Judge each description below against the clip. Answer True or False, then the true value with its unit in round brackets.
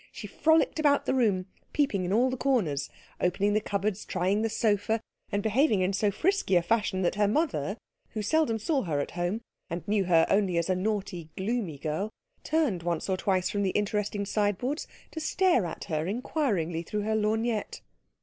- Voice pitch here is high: True (205 Hz)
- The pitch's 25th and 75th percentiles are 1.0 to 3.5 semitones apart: False (4.0 semitones)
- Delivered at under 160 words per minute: False (190 wpm)